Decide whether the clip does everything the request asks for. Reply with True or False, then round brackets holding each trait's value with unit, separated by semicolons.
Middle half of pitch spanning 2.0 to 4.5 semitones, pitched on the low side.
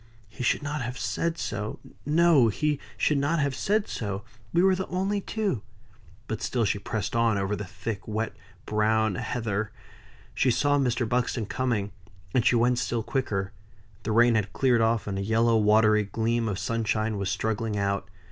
True (3.7 semitones; 115 Hz)